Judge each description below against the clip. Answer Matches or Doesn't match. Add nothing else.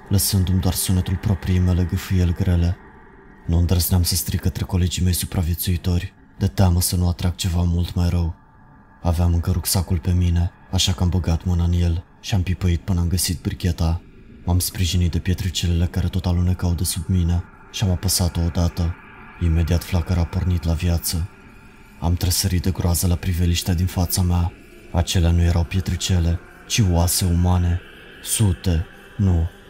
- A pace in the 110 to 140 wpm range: Doesn't match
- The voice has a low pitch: Matches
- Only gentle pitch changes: Matches